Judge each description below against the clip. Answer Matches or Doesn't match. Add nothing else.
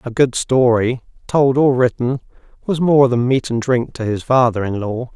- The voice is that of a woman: Doesn't match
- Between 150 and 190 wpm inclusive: Doesn't match